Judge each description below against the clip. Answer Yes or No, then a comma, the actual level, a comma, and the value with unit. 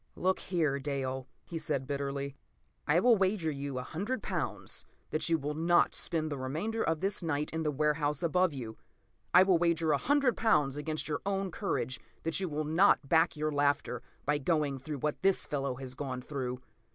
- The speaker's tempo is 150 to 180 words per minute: No, average, 195 wpm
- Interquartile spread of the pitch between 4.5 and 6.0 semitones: No, average, 3.8 semitones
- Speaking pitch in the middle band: Yes, medium, 150 Hz